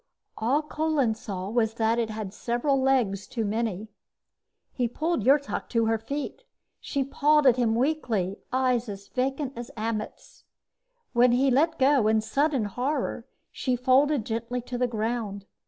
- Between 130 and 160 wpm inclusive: Yes, average, 155 wpm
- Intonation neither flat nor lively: Yes, average, 3.6 semitones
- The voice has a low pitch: No, high, 245 Hz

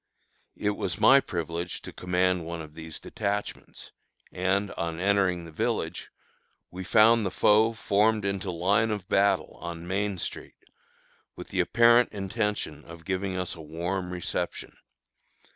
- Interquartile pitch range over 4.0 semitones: No, average, 3.2 semitones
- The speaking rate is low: No, average, 145 wpm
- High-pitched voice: No, very low, 95 Hz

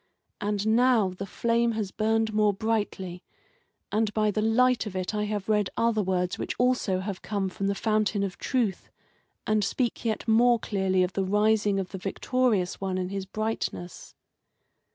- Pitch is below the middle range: No, high, 210 Hz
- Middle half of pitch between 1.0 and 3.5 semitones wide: Yes, narrow, 2.6 semitones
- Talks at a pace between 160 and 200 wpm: Yes, average, 175 wpm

